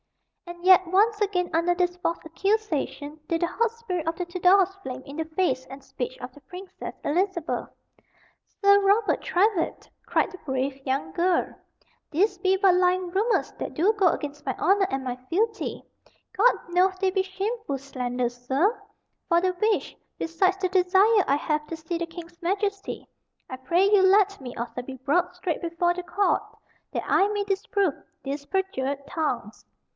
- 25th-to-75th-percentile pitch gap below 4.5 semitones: No, average, 4.8 semitones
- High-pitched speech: Yes, very high, 355 Hz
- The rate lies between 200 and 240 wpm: No, average, 170 wpm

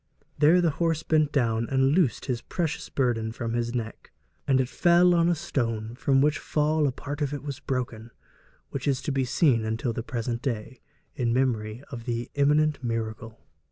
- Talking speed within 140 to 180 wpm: No, average, 190 wpm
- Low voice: Yes, low, 130 Hz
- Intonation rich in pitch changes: No, average, 4.1 semitones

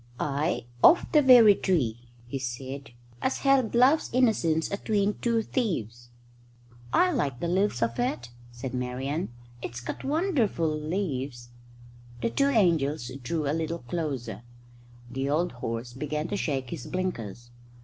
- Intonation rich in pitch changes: Yes, wide, 8.7 semitones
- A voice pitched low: No, medium, 150 Hz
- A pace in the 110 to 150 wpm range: Yes, average, 140 wpm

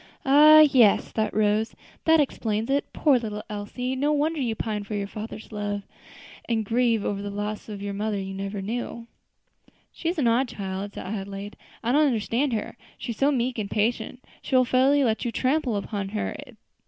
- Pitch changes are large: No, average, 4.0 semitones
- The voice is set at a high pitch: Yes, high, 225 Hz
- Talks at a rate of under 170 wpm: No, average, 190 wpm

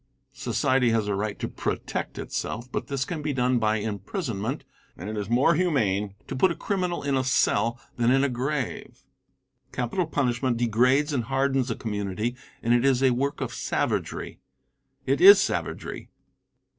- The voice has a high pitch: No, low, 125 Hz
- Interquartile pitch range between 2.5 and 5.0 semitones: Yes, average, 3.5 semitones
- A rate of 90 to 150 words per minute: No, average, 170 wpm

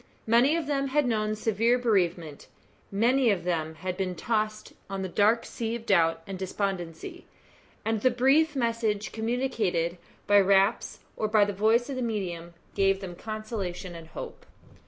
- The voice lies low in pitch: No, high, 210 Hz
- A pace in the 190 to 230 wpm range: No, average, 160 wpm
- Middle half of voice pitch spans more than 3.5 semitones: Yes, average, 4.1 semitones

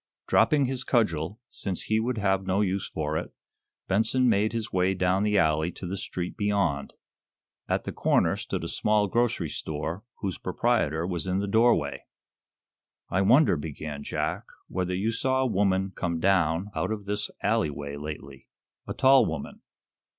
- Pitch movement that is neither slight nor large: Yes, average, 4.4 semitones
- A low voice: Yes, very low, 95 Hz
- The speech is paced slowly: No, average, 165 wpm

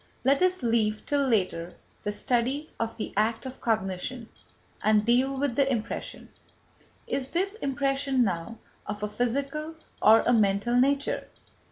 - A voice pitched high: Yes, high, 245 Hz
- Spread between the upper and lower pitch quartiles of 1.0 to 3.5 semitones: No, average, 4.3 semitones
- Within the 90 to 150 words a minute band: Yes, average, 145 wpm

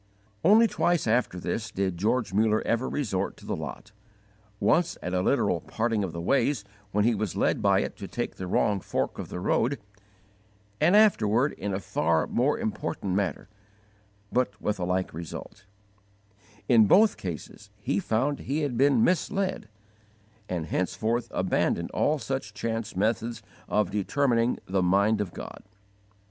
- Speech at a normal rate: Yes, average, 155 wpm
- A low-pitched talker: Yes, low, 110 Hz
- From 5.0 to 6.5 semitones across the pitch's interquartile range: Yes, average, 5.3 semitones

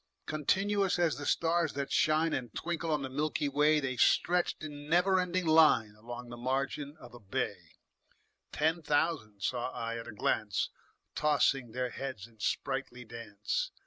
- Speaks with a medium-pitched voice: Yes, medium, 145 Hz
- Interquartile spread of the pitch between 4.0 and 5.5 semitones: Yes, average, 5.0 semitones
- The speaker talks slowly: No, average, 160 wpm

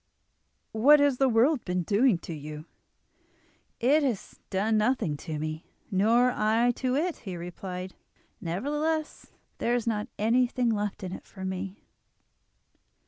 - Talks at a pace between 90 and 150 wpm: Yes, average, 140 wpm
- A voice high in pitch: Yes, high, 220 Hz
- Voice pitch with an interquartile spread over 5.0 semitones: Yes, wide, 5.4 semitones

